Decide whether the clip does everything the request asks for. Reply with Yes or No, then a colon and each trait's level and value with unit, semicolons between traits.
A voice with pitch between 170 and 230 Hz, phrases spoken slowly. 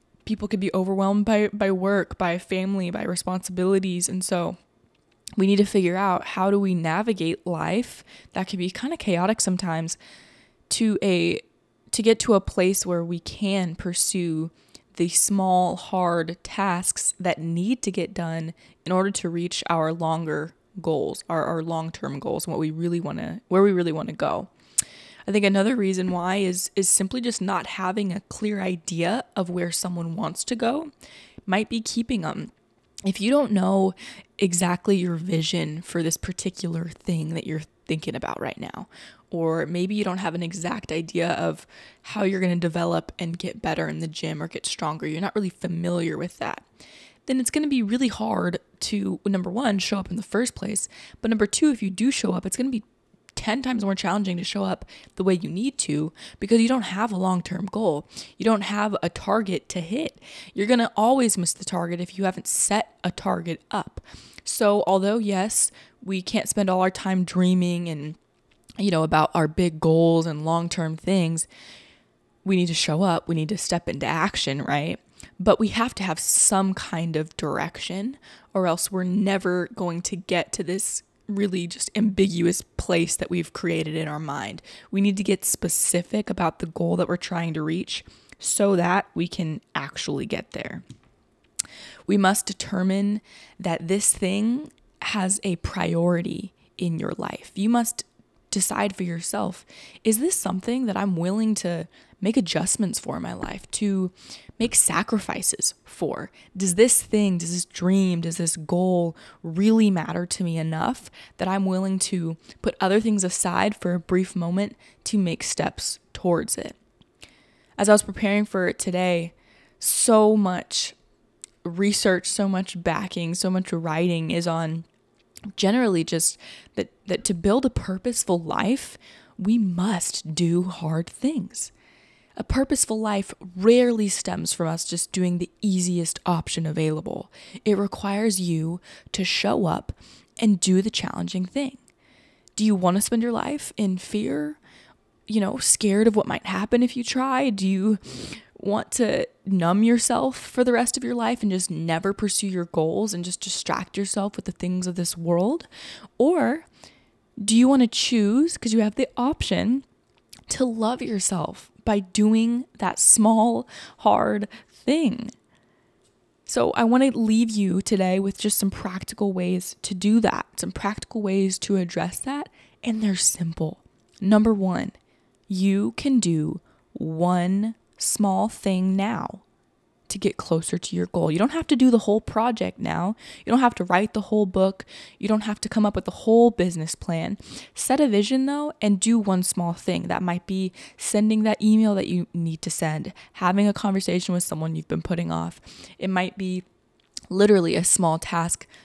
No: high, 190 Hz; average, 175 wpm